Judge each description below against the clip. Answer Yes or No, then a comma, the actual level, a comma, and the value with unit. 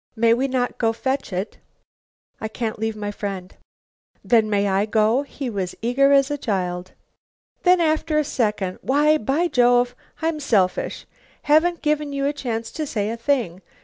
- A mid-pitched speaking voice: No, high, 245 Hz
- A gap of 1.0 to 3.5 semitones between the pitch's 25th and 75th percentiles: No, average, 5.3 semitones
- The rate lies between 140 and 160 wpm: No, average, 170 wpm